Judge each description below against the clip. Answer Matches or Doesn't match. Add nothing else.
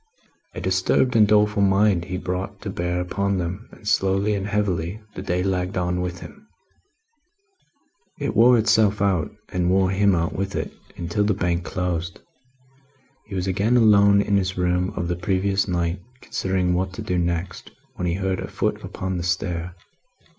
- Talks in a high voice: Doesn't match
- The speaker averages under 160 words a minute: Doesn't match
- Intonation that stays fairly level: Matches